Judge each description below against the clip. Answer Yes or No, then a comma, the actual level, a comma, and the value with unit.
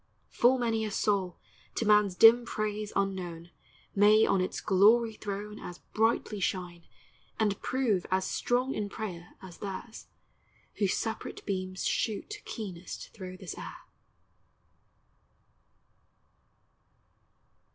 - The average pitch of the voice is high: Yes, high, 205 Hz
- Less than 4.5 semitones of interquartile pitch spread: Yes, average, 3.0 semitones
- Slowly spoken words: Yes, slow, 110 wpm